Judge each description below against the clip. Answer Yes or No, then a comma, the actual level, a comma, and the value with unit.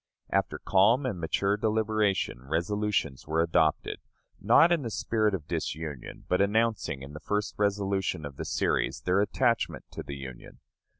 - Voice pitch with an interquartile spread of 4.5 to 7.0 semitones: Yes, average, 5.2 semitones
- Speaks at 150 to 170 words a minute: Yes, average, 155 wpm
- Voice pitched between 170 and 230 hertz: No, low, 100 Hz